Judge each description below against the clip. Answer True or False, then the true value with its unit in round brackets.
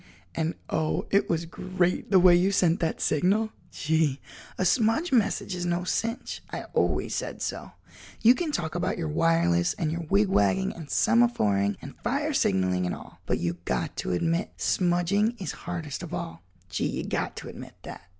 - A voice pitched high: False (170 Hz)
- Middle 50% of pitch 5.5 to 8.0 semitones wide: True (6.8 semitones)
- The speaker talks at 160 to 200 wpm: True (170 wpm)